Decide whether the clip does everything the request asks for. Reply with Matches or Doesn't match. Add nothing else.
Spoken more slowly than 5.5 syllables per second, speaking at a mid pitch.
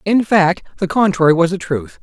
Matches